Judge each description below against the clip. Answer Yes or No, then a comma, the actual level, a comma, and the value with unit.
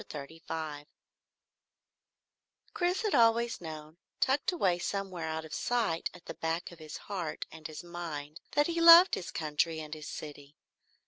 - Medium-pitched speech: Yes, medium, 165 Hz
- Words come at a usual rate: Yes, average, 155 wpm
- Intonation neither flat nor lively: No, wide, 6.5 semitones